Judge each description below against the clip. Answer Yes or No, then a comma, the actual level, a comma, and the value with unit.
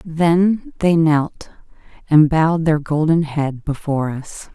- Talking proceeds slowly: Yes, slow, 130 wpm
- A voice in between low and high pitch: Yes, medium, 160 Hz